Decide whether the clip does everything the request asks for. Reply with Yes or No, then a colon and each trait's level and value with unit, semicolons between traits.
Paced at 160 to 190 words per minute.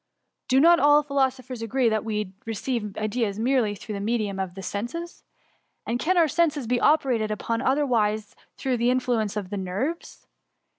Yes: average, 170 wpm